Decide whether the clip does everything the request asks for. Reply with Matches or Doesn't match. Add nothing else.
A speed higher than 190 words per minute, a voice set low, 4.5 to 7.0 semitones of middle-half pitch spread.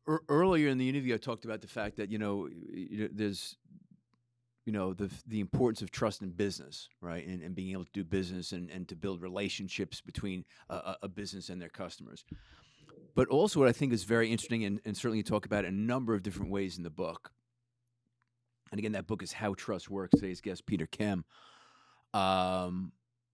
Doesn't match